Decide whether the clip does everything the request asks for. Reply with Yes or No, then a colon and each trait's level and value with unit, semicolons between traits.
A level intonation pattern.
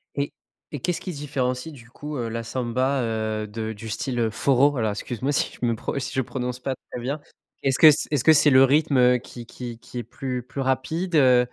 No: average, 3.0 semitones